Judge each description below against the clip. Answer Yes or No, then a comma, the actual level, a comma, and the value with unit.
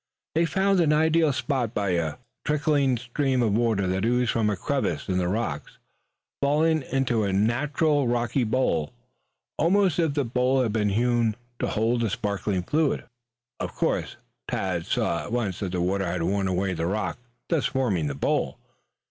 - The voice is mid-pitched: No, low, 120 Hz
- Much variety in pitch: Yes, wide, 6.4 semitones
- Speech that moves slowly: No, average, 175 wpm